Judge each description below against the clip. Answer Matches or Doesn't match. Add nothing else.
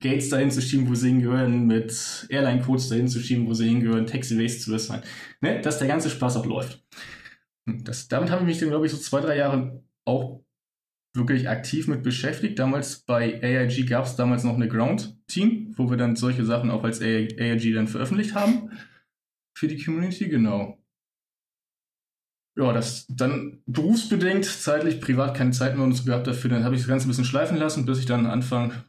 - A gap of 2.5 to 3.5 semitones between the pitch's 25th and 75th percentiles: Matches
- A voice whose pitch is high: Doesn't match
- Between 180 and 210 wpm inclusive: Matches